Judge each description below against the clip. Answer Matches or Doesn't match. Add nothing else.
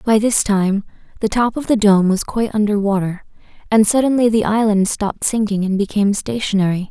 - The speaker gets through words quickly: Doesn't match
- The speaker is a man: Doesn't match